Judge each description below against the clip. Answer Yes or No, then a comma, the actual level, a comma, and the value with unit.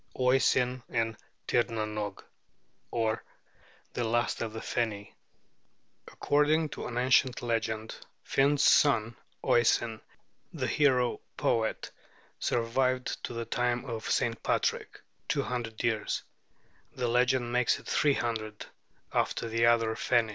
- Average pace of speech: No, slow, 120 wpm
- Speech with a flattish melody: Yes, narrow, 2.0 semitones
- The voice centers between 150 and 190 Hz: No, low, 120 Hz